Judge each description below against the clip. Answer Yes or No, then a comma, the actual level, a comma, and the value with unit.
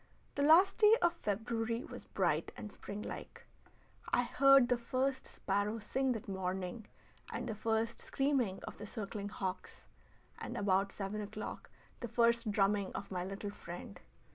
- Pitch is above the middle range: Yes, high, 215 Hz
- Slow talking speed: No, average, 150 wpm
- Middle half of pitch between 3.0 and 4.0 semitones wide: Yes, average, 3.7 semitones